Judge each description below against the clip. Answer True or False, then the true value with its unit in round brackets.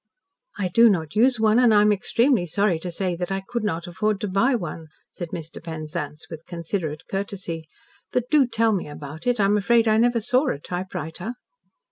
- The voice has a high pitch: True (195 Hz)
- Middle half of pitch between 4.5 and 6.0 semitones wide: True (5.2 semitones)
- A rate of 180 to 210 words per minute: True (200 wpm)